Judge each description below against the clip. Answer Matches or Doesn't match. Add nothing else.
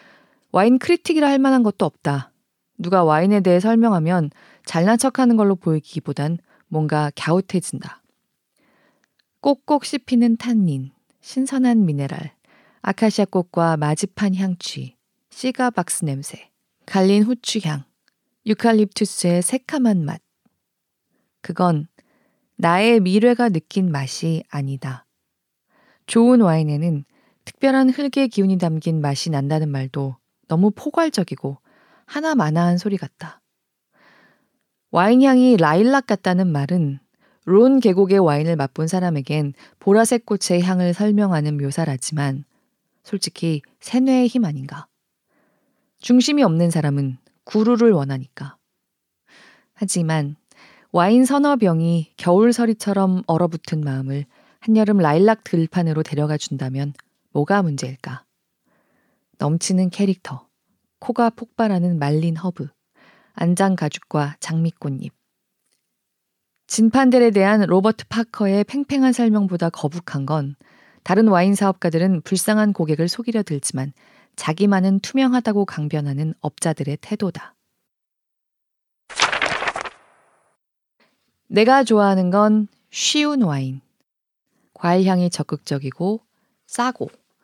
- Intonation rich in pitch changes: Matches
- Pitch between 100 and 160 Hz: Doesn't match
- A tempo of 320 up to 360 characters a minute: Doesn't match